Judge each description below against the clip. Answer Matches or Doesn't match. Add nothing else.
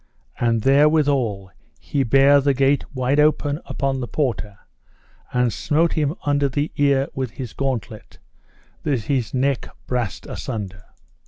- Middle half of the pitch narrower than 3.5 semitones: Matches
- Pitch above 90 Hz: Matches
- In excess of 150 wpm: Doesn't match